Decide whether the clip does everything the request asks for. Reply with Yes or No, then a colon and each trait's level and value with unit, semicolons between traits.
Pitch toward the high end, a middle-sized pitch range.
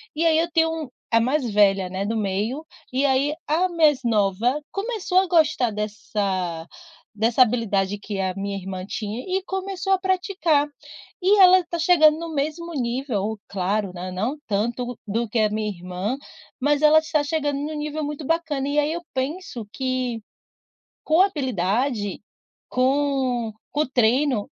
No: very high, 260 Hz; wide, 6.8 semitones